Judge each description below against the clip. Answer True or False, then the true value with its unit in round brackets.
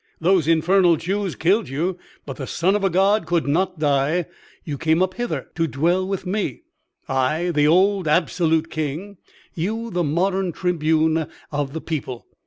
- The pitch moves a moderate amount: True (3.5 semitones)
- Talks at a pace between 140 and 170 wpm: True (165 wpm)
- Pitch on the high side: False (170 Hz)